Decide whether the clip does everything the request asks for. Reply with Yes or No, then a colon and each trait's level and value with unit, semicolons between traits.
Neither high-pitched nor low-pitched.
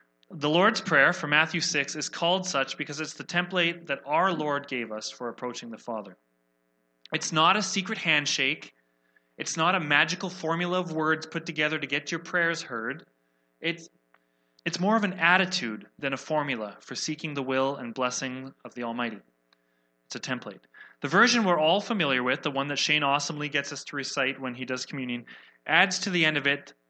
Yes: medium, 145 Hz